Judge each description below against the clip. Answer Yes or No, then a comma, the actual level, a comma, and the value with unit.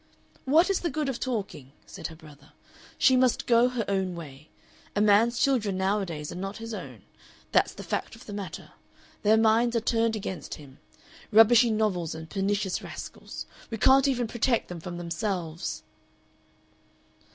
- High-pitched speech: Yes, high, 210 Hz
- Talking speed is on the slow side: No, average, 165 wpm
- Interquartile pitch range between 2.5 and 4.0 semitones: No, average, 5.1 semitones